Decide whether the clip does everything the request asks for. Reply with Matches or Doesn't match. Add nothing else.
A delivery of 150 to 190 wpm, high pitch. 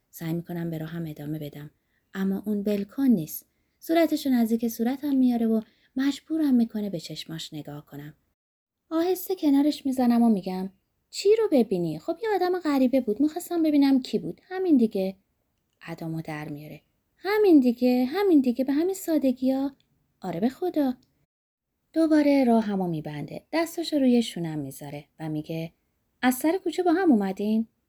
Matches